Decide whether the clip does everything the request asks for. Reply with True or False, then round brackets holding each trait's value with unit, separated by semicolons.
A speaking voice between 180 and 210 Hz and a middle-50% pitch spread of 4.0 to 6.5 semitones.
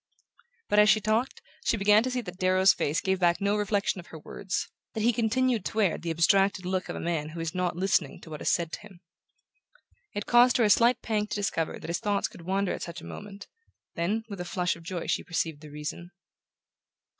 False (190 Hz; 3.4 semitones)